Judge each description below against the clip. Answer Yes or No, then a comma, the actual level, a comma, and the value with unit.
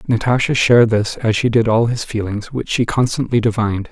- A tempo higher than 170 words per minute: Yes, average, 200 wpm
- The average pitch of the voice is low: Yes, low, 115 Hz